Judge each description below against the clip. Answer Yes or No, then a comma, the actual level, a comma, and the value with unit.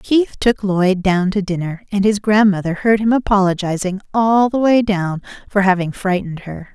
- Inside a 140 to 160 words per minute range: No, average, 180 wpm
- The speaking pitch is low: No, high, 200 Hz